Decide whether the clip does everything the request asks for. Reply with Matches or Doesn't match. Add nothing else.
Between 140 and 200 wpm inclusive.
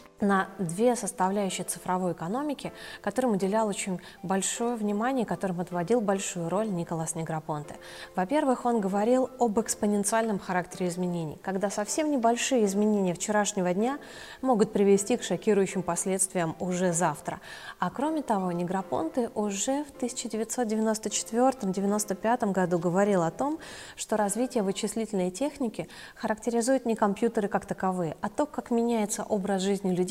Doesn't match